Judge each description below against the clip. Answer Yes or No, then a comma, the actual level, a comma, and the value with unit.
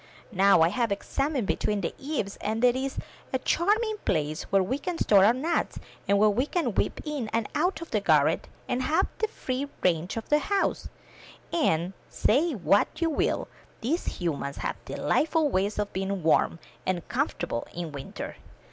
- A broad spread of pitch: Yes, wide, 8.0 semitones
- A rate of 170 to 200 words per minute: Yes, average, 175 wpm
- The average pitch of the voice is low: No, high, 225 Hz